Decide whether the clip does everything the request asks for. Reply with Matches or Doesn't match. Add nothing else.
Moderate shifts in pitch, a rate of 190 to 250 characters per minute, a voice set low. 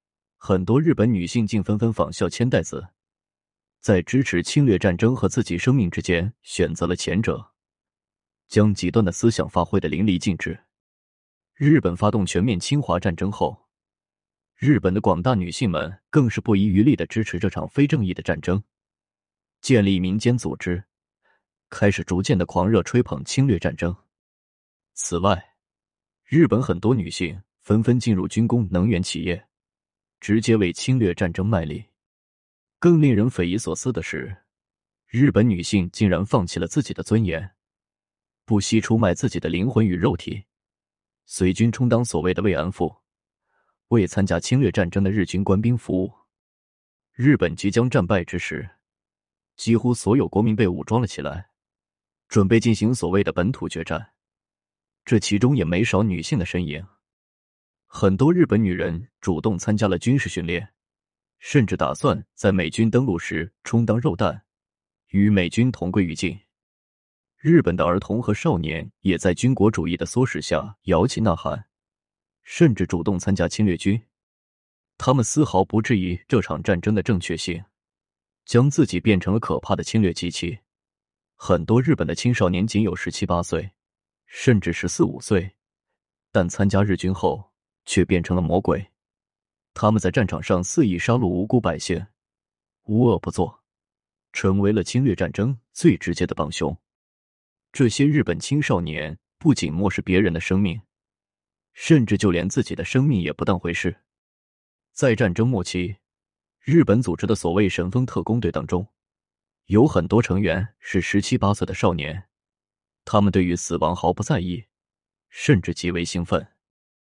Matches